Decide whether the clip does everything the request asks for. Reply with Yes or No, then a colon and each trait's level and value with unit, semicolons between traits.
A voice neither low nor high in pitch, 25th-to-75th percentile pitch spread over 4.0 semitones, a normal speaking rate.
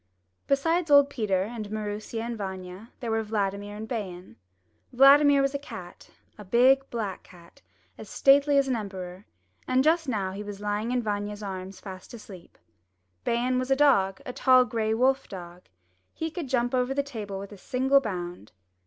No: high, 220 Hz; average, 5.2 semitones; average, 175 wpm